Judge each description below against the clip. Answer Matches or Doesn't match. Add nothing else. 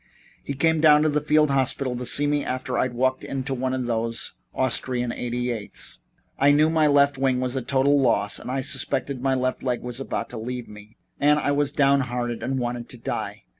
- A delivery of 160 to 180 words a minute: Doesn't match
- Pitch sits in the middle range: Doesn't match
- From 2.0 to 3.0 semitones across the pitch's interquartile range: Matches